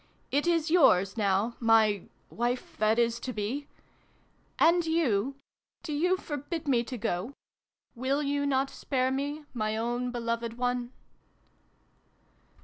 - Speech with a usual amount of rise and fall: Yes, average, 4.0 semitones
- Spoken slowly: Yes, slow, 130 wpm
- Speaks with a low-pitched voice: No, very high, 250 Hz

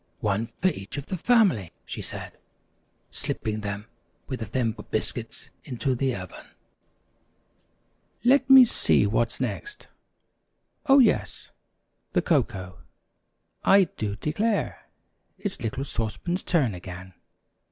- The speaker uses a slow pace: Yes, slow, 120 wpm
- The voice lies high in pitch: No, low, 125 Hz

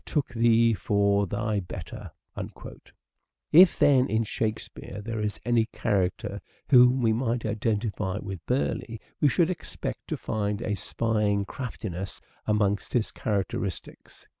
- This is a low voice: Yes, low, 110 Hz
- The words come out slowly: Yes, slow, 125 wpm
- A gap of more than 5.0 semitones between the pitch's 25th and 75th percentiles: No, narrow, 2.5 semitones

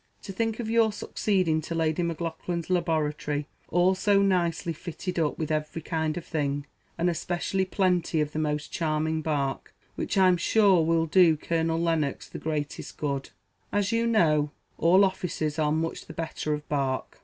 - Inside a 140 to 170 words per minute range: Yes, average, 165 wpm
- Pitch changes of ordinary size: Yes, average, 3.1 semitones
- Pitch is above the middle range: No, medium, 165 Hz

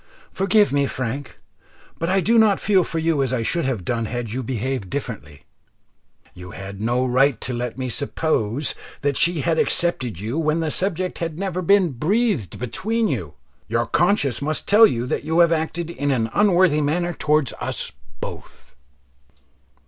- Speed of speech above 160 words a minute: Yes, average, 170 wpm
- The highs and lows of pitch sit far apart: Yes, wide, 6.1 semitones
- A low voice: No, medium, 145 Hz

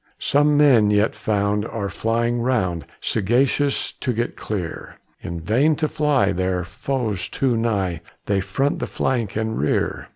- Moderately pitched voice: No, low, 110 Hz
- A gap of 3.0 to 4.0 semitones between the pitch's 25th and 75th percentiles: No, average, 5.0 semitones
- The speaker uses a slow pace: No, average, 150 wpm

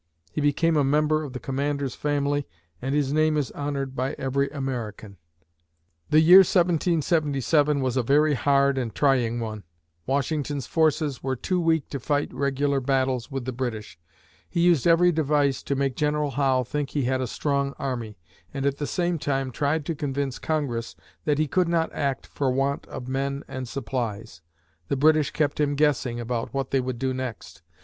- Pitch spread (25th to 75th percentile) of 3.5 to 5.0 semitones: No, narrow, 2.4 semitones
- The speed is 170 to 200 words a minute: Yes, average, 180 wpm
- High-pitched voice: No, medium, 140 Hz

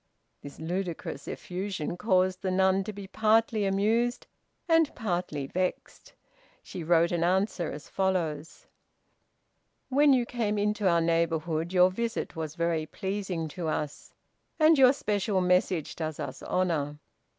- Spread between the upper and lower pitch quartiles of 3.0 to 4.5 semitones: Yes, average, 3.9 semitones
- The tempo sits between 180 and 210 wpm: No, slow, 135 wpm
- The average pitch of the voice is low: No, medium, 185 Hz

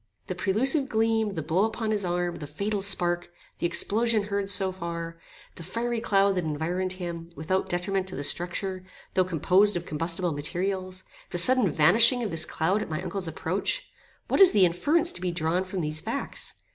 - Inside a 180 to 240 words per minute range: Yes, average, 185 wpm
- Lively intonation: No, average, 3.2 semitones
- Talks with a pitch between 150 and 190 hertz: Yes, medium, 185 Hz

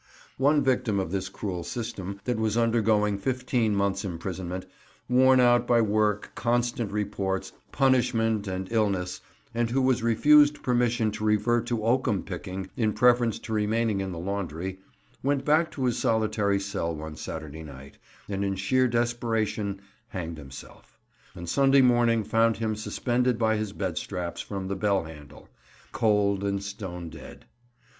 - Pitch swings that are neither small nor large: Yes, average, 3.7 semitones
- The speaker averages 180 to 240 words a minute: No, average, 150 wpm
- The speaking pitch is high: No, low, 105 Hz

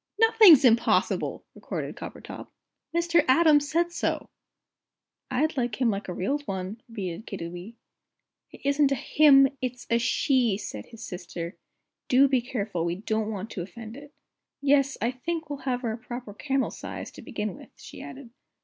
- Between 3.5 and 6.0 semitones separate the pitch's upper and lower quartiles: Yes, average, 5.0 semitones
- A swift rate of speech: No, average, 165 wpm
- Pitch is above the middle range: Yes, high, 245 Hz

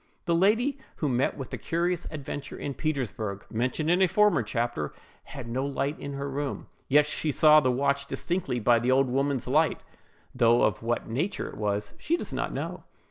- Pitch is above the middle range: No, medium, 140 Hz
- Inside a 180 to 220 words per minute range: Yes, average, 190 wpm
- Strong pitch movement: No, average, 4.6 semitones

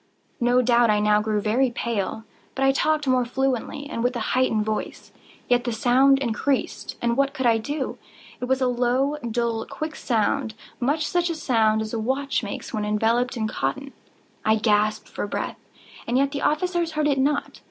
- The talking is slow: No, average, 175 wpm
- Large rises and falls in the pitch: No, average, 3.8 semitones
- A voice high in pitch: Yes, high, 245 Hz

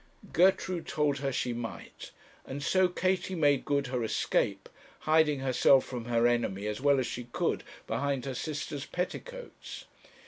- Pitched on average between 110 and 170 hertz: Yes, medium, 140 Hz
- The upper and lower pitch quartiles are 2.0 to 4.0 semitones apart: No, average, 4.5 semitones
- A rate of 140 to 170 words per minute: Yes, average, 150 wpm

